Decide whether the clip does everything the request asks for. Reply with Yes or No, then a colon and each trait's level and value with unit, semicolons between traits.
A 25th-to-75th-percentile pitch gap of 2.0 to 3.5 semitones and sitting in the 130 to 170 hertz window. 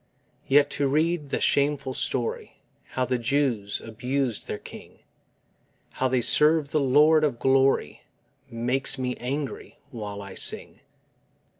Yes: average, 2.8 semitones; low, 135 Hz